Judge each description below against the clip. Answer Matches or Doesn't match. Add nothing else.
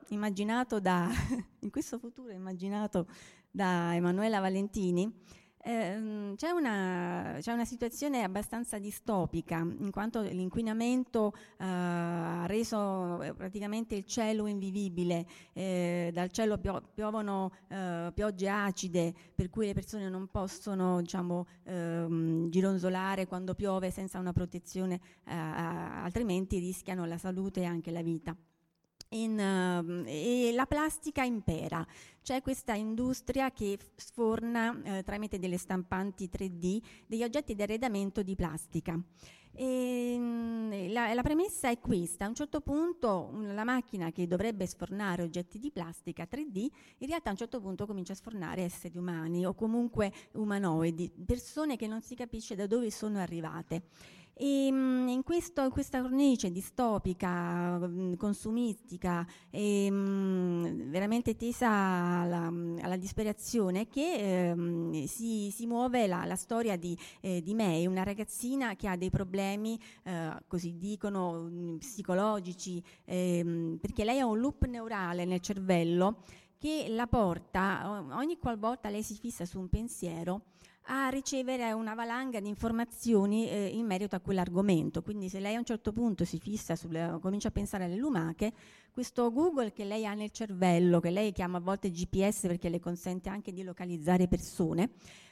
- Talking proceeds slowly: Doesn't match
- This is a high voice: Matches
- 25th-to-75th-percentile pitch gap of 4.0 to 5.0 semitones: Matches